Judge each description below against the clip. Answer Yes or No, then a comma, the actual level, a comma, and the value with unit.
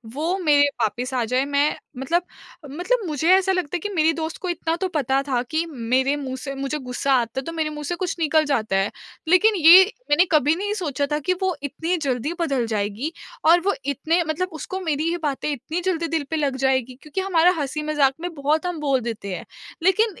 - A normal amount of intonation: Yes, average, 4.2 semitones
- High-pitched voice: Yes, very high, 305 Hz